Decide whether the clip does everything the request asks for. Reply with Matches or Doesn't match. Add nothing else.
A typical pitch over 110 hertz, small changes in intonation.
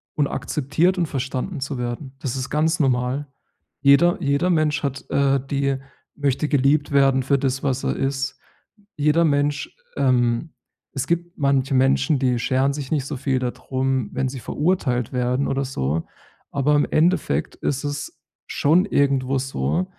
Matches